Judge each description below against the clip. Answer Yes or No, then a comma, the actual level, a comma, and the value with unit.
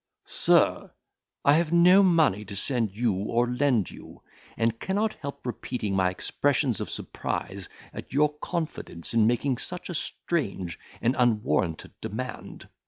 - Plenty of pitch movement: Yes, wide, 6.4 semitones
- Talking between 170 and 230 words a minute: No, average, 140 wpm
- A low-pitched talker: Yes, low, 125 Hz